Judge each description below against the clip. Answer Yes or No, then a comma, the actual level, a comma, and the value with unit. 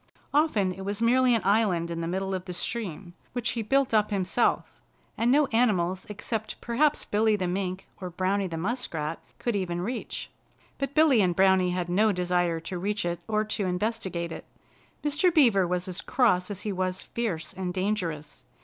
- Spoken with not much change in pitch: No, average, 4.1 semitones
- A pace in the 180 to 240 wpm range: Yes, average, 185 wpm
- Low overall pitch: No, high, 195 Hz